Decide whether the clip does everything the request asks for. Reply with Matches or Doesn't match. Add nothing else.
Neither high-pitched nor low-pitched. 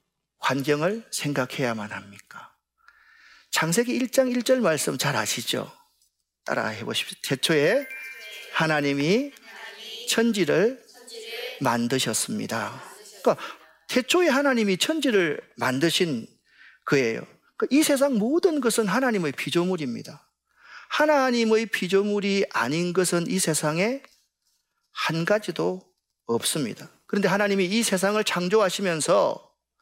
Doesn't match